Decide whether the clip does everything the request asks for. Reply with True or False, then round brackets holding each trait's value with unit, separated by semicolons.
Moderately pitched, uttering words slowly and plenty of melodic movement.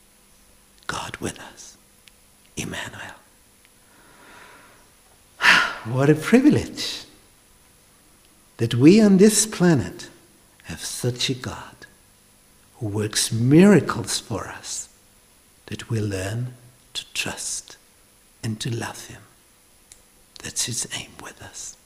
False (120 Hz; 95 wpm; 6.4 semitones)